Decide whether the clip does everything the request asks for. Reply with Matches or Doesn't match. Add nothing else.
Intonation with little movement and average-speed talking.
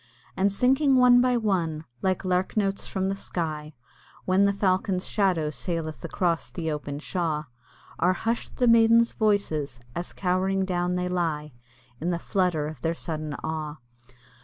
Doesn't match